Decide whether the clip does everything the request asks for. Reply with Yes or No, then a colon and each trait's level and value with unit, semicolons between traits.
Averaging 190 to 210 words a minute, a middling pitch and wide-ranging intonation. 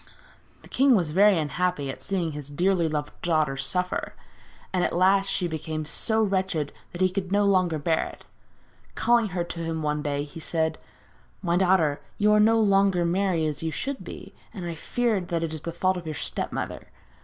No: average, 200 wpm; medium, 175 Hz; average, 3.7 semitones